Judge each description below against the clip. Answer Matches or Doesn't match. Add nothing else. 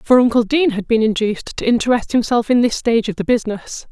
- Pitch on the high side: Matches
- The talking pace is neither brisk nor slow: Doesn't match